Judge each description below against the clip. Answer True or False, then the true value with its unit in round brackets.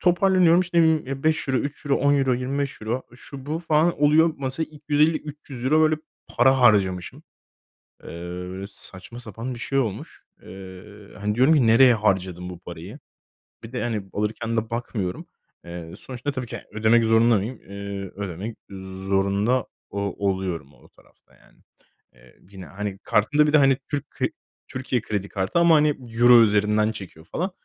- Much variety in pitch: True (6.2 semitones)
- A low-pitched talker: True (115 Hz)